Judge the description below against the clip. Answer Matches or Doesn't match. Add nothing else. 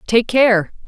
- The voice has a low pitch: Doesn't match